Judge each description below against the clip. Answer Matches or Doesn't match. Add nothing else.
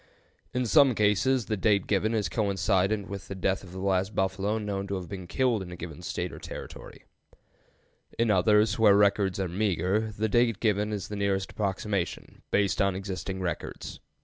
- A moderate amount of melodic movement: Doesn't match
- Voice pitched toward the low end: Matches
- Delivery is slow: Doesn't match